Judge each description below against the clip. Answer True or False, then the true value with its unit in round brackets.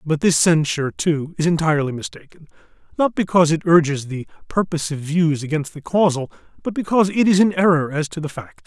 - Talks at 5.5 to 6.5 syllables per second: True (6.1 syllables/s)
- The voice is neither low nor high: True (165 Hz)